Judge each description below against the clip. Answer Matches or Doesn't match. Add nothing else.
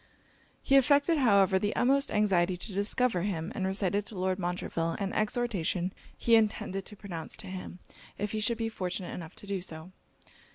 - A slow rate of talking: Doesn't match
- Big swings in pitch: Doesn't match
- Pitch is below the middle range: Doesn't match